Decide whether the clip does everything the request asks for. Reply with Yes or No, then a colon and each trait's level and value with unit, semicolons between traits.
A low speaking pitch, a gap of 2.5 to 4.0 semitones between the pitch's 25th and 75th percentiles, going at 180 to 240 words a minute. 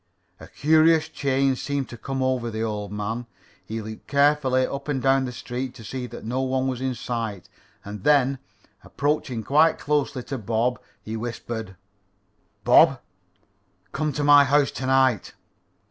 No: low, 130 Hz; average, 3.6 semitones; average, 160 wpm